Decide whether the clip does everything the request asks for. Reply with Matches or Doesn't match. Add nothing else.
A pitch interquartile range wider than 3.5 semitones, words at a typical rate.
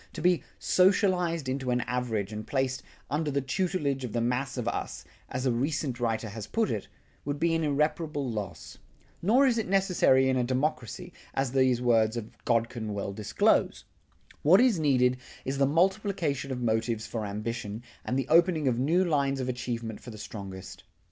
Matches